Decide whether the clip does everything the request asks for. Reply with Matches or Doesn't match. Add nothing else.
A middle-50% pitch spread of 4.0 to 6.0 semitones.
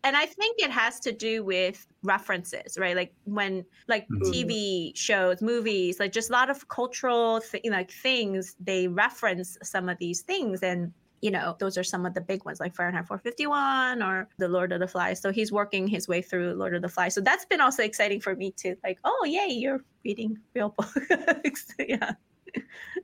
Matches